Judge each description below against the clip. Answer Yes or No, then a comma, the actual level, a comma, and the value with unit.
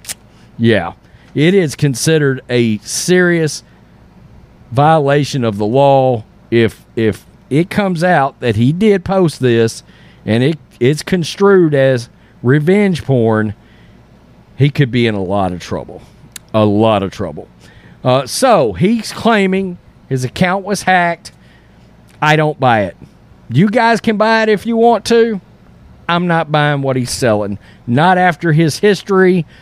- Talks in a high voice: No, medium, 140 Hz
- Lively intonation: Yes, wide, 8.1 semitones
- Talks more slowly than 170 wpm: Yes, average, 140 wpm